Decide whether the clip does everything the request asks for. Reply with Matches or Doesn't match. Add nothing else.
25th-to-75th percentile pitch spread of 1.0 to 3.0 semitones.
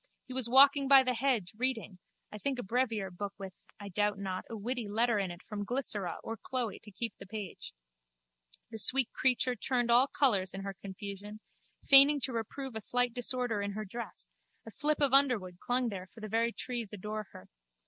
Doesn't match